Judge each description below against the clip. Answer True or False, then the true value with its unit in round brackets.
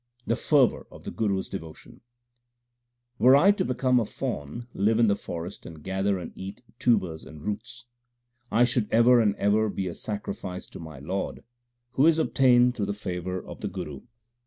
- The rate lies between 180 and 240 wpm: True (185 wpm)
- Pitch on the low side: True (100 Hz)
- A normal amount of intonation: True (4.8 semitones)